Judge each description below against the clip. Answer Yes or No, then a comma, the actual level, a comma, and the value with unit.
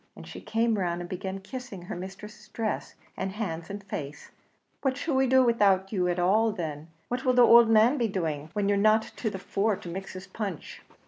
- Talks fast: Yes, fast, 215 wpm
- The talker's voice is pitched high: Yes, high, 200 Hz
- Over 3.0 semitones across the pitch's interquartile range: Yes, average, 3.6 semitones